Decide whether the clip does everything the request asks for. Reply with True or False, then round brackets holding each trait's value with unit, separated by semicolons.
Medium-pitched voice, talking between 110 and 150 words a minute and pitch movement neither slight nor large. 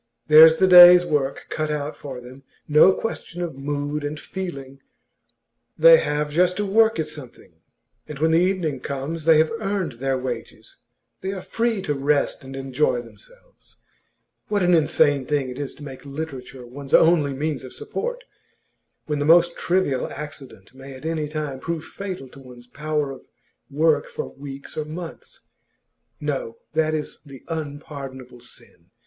False (150 Hz; 165 wpm; 3.7 semitones)